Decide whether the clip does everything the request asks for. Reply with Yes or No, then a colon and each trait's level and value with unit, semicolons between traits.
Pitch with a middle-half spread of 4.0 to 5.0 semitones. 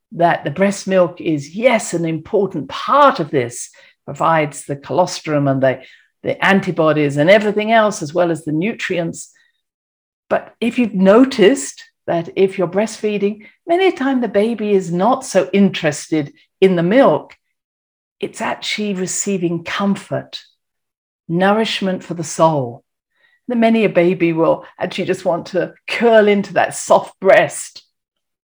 Yes: average, 4.5 semitones